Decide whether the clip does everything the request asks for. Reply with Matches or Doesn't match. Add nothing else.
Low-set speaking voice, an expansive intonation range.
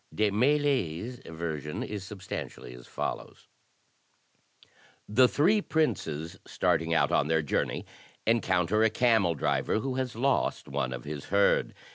Matches